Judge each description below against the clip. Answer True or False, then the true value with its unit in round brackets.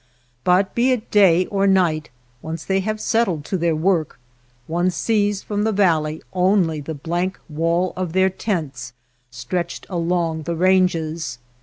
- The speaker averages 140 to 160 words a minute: True (150 wpm)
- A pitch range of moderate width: True (3.2 semitones)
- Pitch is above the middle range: False (180 Hz)